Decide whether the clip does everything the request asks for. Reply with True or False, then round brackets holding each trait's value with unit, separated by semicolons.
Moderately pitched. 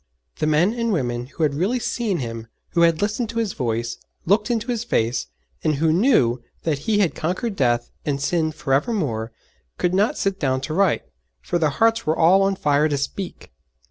True (165 Hz)